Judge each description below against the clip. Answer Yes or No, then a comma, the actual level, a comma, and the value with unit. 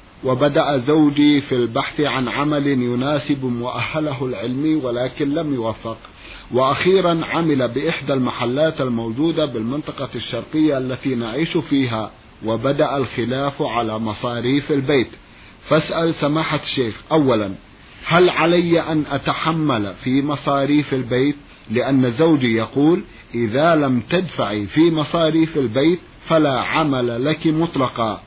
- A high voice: No, medium, 140 Hz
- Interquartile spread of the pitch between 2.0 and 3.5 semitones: No, average, 4.2 semitones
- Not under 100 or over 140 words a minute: Yes, average, 110 wpm